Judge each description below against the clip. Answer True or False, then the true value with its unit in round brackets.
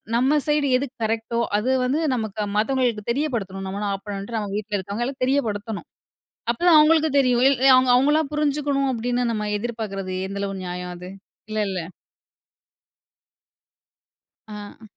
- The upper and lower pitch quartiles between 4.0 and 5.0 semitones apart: True (4.7 semitones)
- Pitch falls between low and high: False (225 Hz)